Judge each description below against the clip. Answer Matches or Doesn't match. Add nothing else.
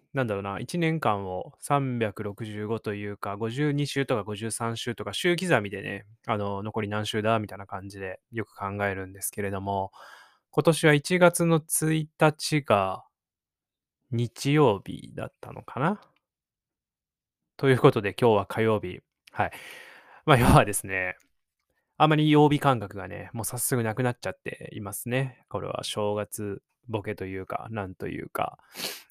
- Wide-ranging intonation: Matches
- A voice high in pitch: Doesn't match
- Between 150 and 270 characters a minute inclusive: Matches